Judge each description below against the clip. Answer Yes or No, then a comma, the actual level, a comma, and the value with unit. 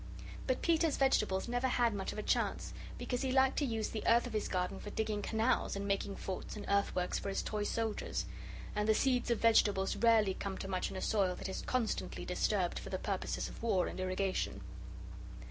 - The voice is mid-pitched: No, high, 215 Hz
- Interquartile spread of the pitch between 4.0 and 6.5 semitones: No, average, 3.5 semitones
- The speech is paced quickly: Yes, fast, 210 wpm